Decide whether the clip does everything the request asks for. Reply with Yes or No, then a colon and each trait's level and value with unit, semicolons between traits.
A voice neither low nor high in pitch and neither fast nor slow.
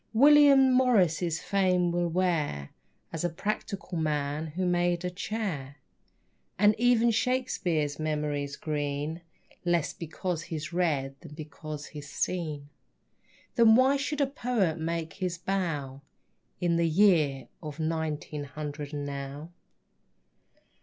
No: medium, 165 Hz; slow, 120 wpm